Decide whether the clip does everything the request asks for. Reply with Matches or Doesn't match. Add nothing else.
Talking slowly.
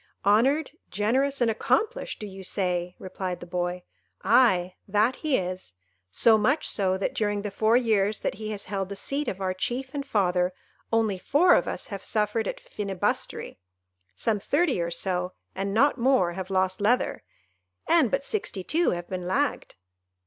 Doesn't match